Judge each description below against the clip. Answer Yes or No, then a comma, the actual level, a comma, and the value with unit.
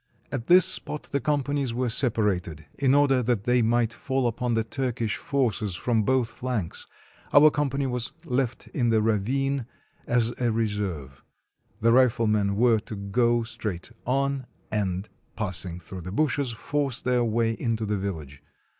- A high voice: No, low, 115 Hz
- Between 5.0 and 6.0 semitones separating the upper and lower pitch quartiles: No, average, 3.8 semitones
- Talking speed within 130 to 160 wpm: Yes, average, 155 wpm